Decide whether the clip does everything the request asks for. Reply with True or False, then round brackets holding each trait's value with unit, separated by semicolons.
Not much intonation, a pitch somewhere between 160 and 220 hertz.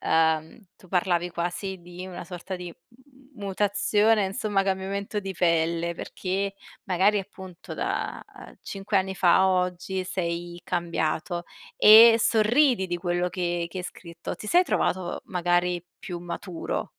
True (2.3 semitones; 185 Hz)